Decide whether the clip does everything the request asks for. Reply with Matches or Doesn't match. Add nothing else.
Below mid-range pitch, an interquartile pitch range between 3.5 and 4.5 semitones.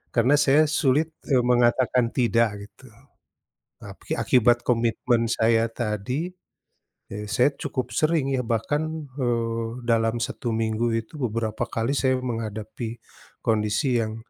Doesn't match